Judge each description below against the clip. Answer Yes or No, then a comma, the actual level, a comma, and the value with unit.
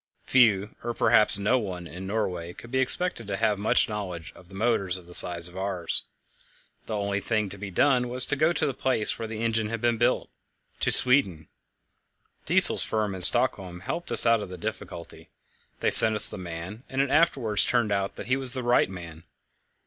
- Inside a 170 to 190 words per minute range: No, average, 200 wpm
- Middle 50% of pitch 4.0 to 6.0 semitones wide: Yes, average, 4.4 semitones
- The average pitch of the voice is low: Yes, low, 105 Hz